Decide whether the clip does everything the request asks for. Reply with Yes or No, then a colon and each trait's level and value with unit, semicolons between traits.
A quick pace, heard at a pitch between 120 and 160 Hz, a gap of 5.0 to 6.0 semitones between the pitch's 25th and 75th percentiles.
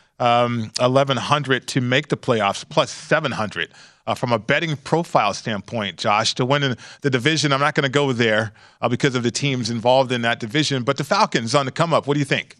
No: fast, 220 wpm; low, 135 Hz; average, 3.3 semitones